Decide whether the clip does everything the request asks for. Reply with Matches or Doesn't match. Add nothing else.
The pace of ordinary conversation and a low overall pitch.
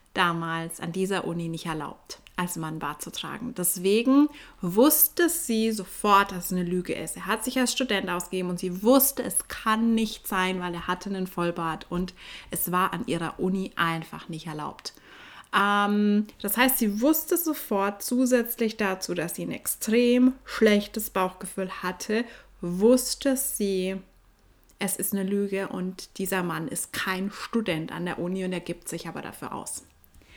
Doesn't match